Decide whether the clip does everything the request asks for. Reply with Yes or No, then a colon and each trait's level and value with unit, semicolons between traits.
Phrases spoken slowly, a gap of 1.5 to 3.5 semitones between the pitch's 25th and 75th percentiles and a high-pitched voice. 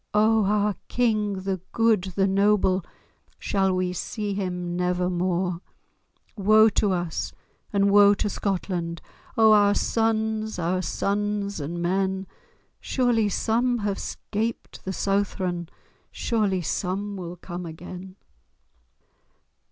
Yes: slow, 115 wpm; narrow, 2.6 semitones; high, 195 Hz